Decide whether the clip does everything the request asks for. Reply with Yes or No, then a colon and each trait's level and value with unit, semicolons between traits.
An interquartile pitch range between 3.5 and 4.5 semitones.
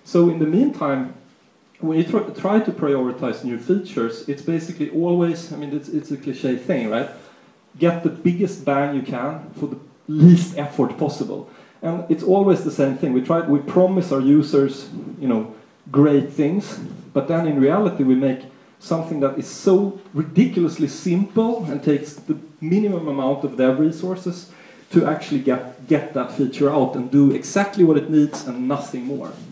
Yes: average, 4.2 semitones